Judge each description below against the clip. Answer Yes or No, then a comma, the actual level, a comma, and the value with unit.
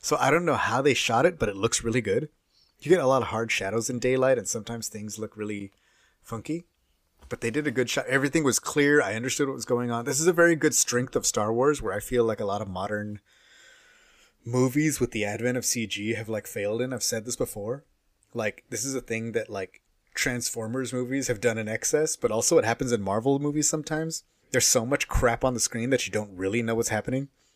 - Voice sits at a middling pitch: No, low, 120 Hz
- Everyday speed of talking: No, fast, 235 wpm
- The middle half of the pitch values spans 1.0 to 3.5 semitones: No, average, 3.9 semitones